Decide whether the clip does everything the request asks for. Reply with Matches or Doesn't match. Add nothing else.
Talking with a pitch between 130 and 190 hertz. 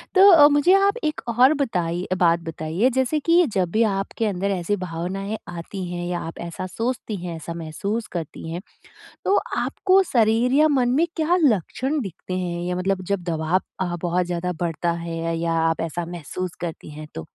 Matches